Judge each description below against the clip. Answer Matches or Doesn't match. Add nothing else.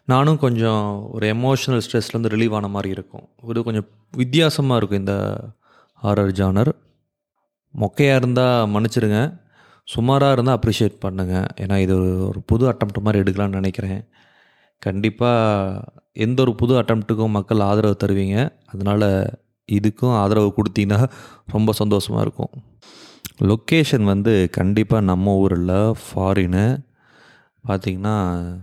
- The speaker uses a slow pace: Matches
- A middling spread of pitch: Matches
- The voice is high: Doesn't match